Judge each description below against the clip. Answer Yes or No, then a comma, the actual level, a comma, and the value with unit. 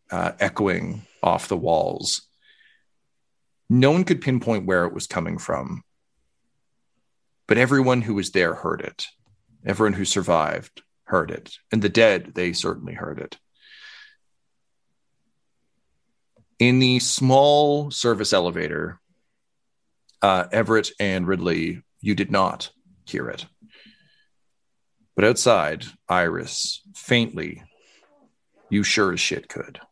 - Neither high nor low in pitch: No, low, 120 Hz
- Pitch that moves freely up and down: Yes, wide, 6.7 semitones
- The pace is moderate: No, slow, 110 wpm